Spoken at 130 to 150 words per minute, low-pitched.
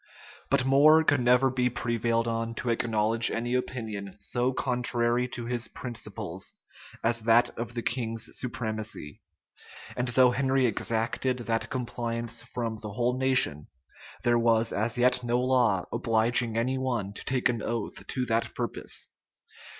Yes: average, 145 wpm; low, 120 Hz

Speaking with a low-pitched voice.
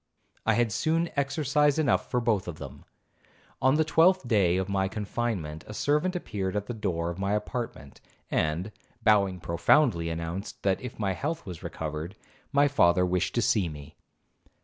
Yes: low, 105 Hz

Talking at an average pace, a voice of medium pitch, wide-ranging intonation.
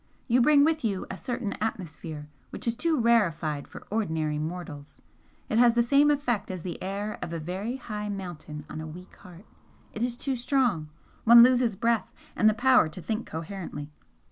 No: average, 185 wpm; high, 210 Hz; wide, 6.3 semitones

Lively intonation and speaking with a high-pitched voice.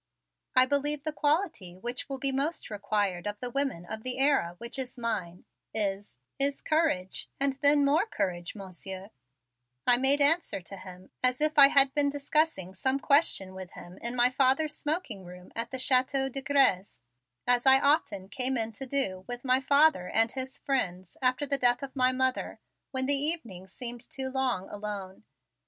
Yes: wide, 6.0 semitones; very high, 255 Hz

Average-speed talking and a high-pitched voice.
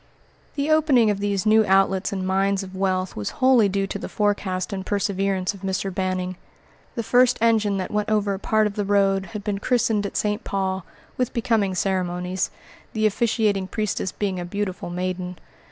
Yes: average, 185 wpm; high, 200 Hz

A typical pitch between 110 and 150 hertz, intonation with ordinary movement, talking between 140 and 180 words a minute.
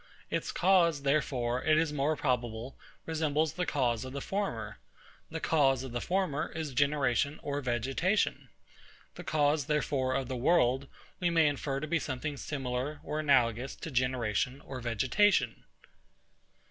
Yes: medium, 140 Hz; average, 3.5 semitones; average, 145 wpm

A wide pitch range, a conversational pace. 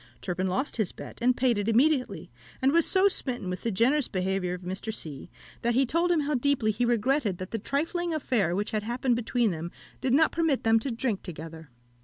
No: wide, 6.2 semitones; fast, 215 wpm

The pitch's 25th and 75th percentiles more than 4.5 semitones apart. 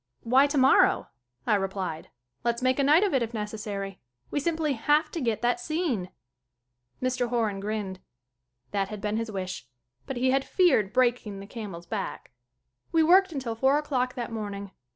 Yes: average, 5.0 semitones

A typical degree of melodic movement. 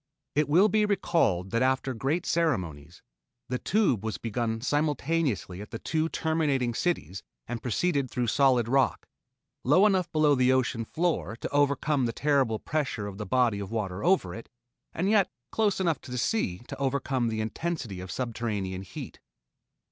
No: wide, 6.1 semitones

